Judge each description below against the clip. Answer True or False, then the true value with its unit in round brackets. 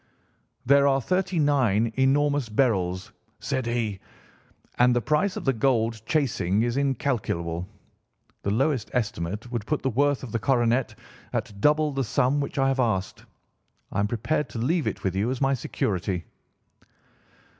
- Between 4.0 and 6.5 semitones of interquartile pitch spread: True (4.8 semitones)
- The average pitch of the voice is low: True (125 Hz)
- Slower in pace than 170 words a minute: True (155 wpm)